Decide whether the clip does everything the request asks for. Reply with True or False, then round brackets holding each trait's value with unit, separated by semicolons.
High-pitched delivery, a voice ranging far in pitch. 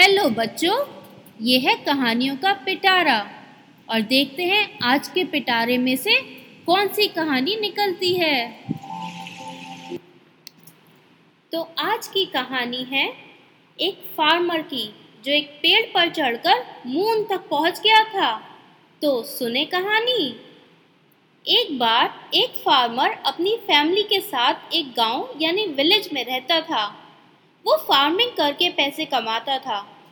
True (310 Hz; 7.4 semitones)